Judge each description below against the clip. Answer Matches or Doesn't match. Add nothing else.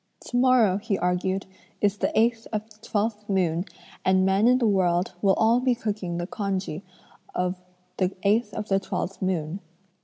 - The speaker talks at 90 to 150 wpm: Doesn't match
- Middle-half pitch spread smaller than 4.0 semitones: Matches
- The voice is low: Doesn't match